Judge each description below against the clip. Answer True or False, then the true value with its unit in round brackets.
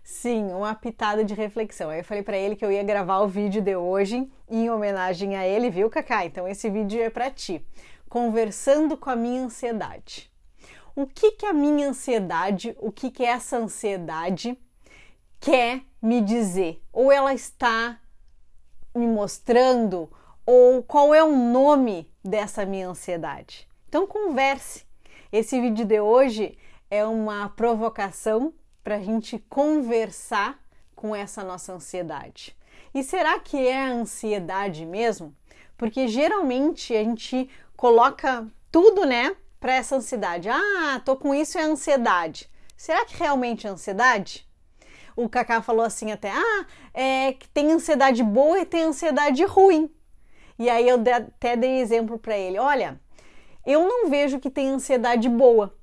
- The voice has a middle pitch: False (235 Hz)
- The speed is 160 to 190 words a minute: False (145 wpm)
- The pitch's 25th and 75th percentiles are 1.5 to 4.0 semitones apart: False (4.6 semitones)